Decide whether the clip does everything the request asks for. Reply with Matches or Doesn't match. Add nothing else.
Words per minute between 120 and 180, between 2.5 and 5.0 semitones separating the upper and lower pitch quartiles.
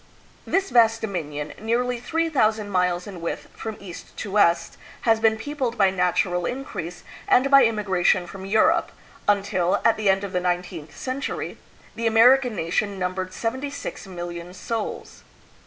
Matches